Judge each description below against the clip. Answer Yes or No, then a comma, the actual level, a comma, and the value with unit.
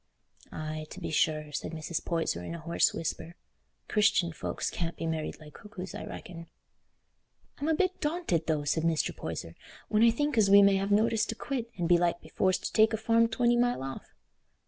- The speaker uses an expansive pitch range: Yes, wide, 5.9 semitones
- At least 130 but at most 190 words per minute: No, average, 200 wpm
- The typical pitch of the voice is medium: Yes, medium, 180 Hz